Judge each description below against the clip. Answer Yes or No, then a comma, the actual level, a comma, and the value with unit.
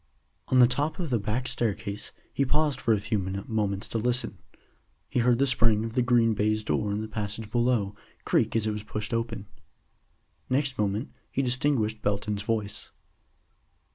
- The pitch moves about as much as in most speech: Yes, average, 3.0 semitones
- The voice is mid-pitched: No, low, 110 Hz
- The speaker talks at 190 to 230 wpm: No, average, 170 wpm